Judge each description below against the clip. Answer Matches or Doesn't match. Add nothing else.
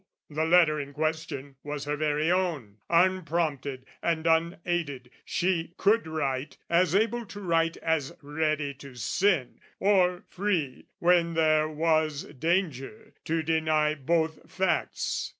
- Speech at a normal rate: Doesn't match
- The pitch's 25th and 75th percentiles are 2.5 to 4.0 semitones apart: Matches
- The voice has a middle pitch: Matches